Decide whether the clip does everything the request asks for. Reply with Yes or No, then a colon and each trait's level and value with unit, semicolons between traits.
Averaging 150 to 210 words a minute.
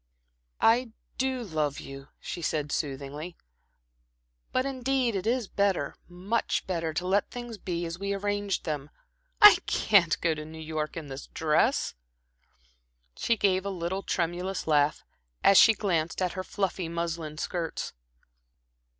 No: average, 140 wpm